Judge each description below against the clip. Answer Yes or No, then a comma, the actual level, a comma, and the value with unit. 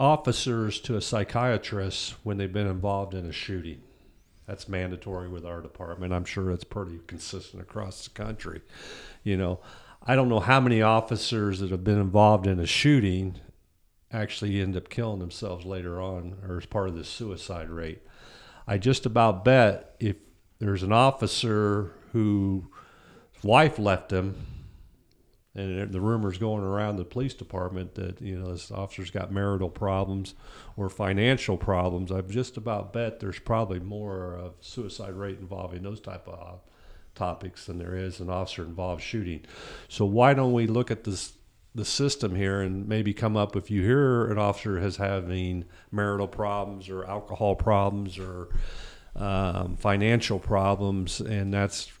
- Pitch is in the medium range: No, low, 100 Hz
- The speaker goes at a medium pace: Yes, average, 165 wpm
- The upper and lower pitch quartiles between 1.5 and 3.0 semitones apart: Yes, average, 2.7 semitones